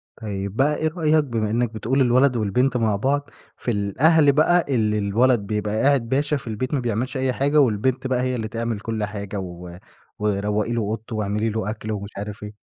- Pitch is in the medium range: No, low, 115 Hz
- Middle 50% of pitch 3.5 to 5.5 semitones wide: Yes, average, 3.9 semitones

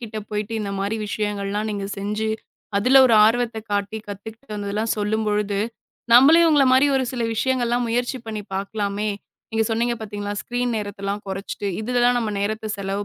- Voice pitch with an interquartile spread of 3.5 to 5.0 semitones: No, average, 2.8 semitones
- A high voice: Yes, high, 215 Hz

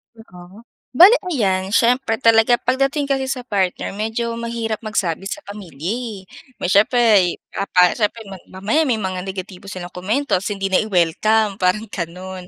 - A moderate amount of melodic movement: Yes, average, 3.9 semitones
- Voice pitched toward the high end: Yes, high, 210 Hz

